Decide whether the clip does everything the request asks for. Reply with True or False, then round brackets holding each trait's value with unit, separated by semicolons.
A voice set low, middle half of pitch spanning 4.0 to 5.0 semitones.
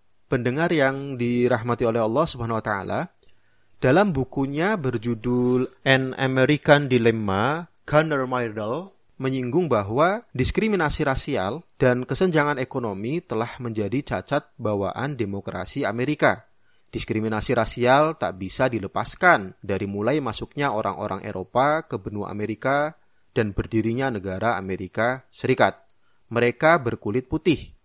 True (125 Hz; 4.4 semitones)